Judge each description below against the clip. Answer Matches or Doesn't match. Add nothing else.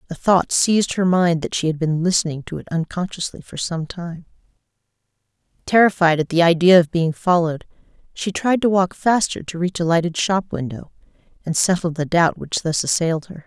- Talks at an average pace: Matches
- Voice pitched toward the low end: Doesn't match